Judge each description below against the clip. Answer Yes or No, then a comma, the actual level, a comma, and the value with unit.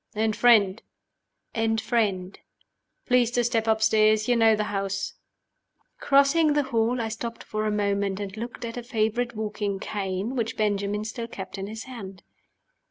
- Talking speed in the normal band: Yes, average, 160 wpm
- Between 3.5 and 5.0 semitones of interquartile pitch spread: No, narrow, 2.4 semitones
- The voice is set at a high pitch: Yes, high, 220 Hz